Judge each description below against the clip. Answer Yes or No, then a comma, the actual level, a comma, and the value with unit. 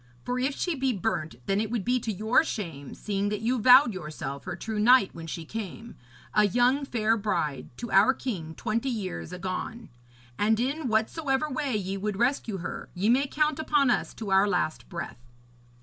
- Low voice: No, high, 220 Hz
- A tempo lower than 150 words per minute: No, average, 190 wpm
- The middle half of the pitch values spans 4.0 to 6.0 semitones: Yes, average, 4.7 semitones